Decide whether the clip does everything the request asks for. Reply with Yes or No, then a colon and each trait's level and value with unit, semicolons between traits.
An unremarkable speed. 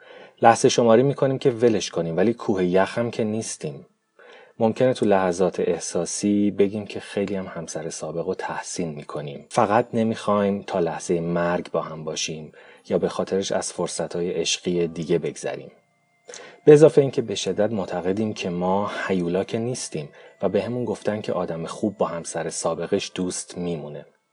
No: fast, 160 wpm